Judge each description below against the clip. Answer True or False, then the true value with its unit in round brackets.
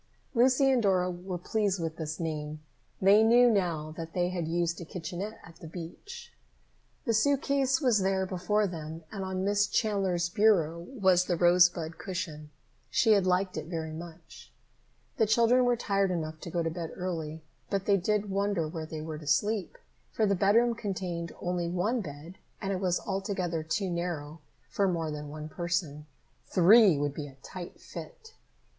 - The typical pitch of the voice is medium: True (180 Hz)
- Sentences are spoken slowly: False (175 wpm)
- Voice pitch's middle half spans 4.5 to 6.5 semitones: False (3.8 semitones)